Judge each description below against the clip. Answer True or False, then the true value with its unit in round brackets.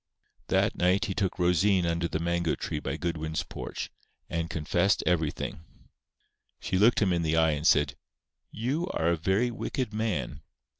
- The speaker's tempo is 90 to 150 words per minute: False (160 wpm)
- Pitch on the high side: False (85 Hz)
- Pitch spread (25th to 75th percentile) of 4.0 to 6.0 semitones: False (3.6 semitones)